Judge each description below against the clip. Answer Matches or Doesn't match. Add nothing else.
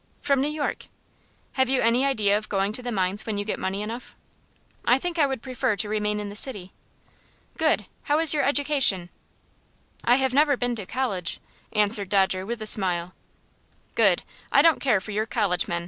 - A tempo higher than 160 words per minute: Matches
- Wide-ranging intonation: Doesn't match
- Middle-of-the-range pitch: Doesn't match